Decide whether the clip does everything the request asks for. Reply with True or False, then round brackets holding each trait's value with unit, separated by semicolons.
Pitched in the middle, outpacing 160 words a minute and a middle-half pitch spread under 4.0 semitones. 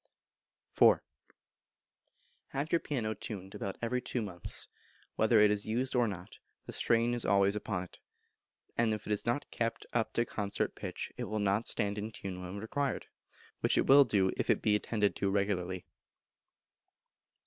False (105 Hz; 170 wpm; 2.9 semitones)